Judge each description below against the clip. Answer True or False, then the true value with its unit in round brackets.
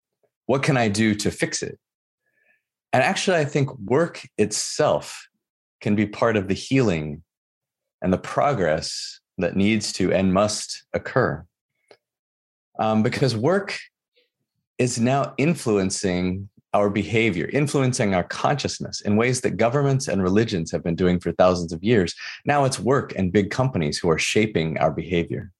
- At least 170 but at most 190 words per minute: False (150 wpm)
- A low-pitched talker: True (105 Hz)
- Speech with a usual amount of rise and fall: False (6.1 semitones)